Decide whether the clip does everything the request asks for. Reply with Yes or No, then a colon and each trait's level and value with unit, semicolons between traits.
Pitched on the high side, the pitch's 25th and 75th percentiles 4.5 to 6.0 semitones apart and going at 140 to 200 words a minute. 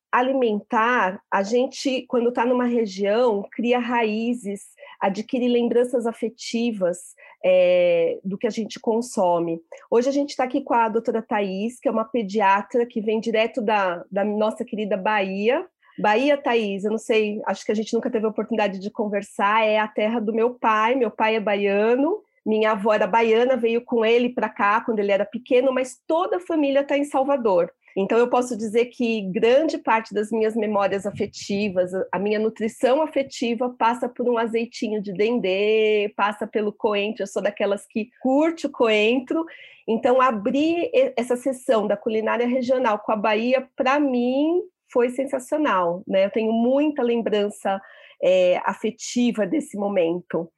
No: high, 230 Hz; average, 3.3 semitones; average, 165 wpm